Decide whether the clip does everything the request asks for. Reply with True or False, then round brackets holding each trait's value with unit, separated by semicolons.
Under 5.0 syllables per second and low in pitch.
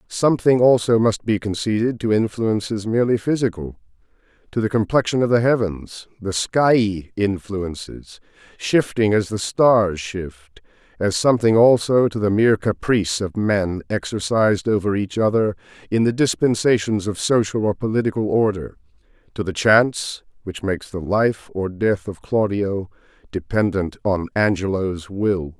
True (4.7 syllables/s; 105 Hz)